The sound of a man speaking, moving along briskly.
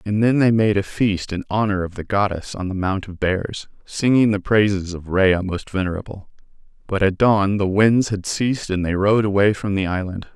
Yes: male; fast, 215 wpm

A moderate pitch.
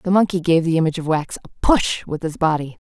Yes: medium, 165 Hz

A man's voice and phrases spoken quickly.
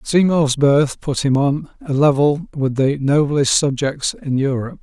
No: male; average, 160 wpm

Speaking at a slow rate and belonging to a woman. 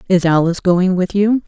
No: fast, 205 wpm; female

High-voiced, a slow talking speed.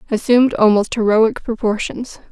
Yes: high, 225 Hz; slow, 105 wpm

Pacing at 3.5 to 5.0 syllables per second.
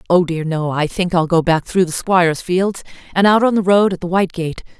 No: 5.5 syllables/s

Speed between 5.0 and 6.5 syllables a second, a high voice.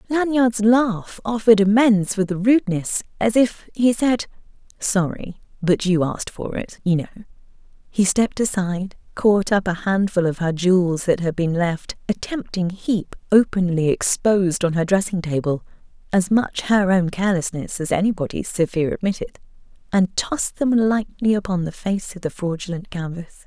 No: 4.3 syllables/s; high, 195 Hz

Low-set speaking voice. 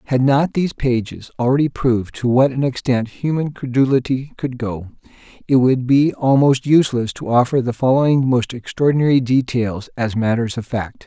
Yes: low, 125 Hz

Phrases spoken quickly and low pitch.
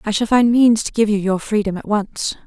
No: fast, 270 wpm; high, 215 Hz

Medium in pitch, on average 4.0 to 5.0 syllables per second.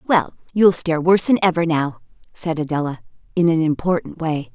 No: medium, 165 Hz; 5.5 syllables/s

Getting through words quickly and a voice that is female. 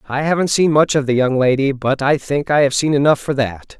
No: fast, 270 wpm; male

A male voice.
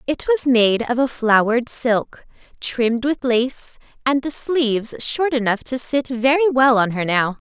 No: female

